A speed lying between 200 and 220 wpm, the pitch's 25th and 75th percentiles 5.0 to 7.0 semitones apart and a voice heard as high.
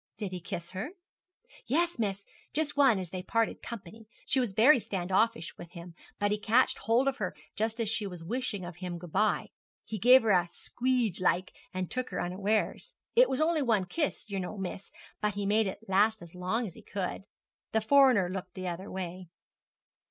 No: fast, 205 wpm; average, 4.1 semitones; high, 205 Hz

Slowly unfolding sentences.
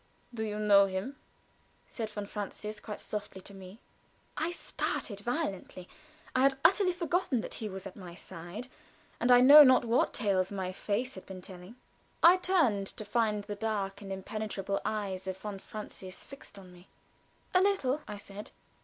No: average, 170 wpm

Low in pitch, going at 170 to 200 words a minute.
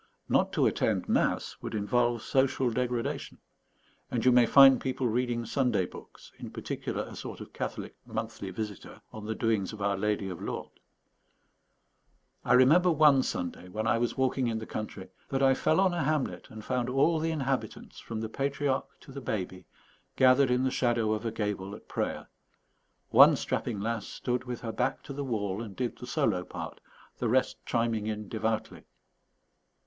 Yes: low, 120 Hz; average, 180 wpm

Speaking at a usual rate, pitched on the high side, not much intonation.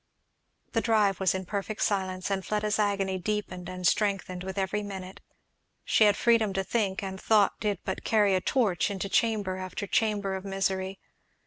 Yes: average, 175 wpm; high, 195 Hz; narrow, 1.9 semitones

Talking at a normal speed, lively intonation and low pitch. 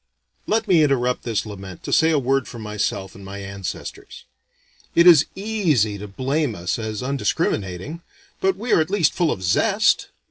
Yes: average, 175 wpm; wide, 8.3 semitones; low, 125 Hz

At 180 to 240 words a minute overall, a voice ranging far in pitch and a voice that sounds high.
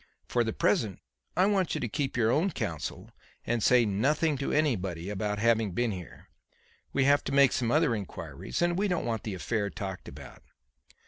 No: average, 190 wpm; wide, 5.8 semitones; low, 120 Hz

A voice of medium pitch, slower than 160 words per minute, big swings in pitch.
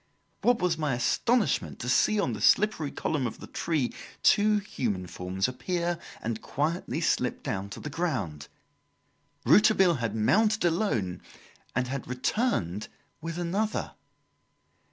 Yes: medium, 150 Hz; slow, 135 wpm; wide, 8.9 semitones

